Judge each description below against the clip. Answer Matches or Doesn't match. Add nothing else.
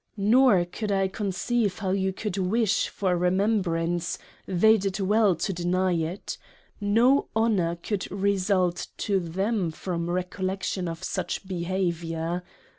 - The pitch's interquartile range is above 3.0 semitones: Doesn't match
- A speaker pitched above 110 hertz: Matches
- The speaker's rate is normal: Doesn't match